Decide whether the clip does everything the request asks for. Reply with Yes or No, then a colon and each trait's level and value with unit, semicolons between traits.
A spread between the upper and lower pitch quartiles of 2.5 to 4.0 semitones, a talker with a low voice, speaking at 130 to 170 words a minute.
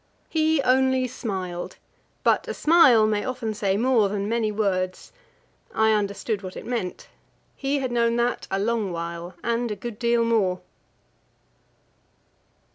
No: average, 3.6 semitones; high, 220 Hz; average, 140 wpm